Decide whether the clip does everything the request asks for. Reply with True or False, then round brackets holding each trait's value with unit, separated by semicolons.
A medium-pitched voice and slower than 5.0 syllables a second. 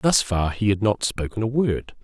False (110 Hz; 4.6 syllables/s)